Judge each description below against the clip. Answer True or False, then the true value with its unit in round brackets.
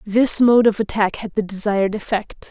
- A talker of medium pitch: False (210 Hz)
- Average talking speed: True (190 wpm)